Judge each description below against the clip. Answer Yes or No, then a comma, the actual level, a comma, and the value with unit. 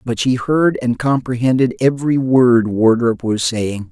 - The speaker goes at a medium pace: Yes, average, 155 wpm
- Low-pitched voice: Yes, low, 120 Hz